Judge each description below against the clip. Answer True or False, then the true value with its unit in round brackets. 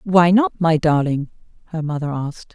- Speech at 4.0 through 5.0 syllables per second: True (4.9 syllables/s)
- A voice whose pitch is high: False (165 Hz)